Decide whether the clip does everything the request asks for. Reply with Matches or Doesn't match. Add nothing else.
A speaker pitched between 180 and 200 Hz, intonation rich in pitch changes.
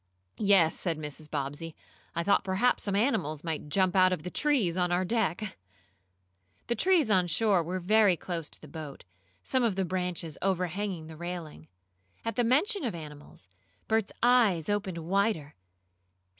Doesn't match